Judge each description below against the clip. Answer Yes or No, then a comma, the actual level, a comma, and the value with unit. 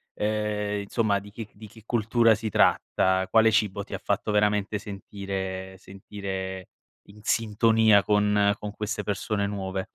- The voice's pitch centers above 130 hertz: No, low, 105 Hz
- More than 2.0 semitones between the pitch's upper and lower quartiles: No, narrow, 1.5 semitones